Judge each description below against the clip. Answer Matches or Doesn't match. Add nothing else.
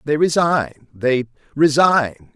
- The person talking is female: Doesn't match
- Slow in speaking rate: Matches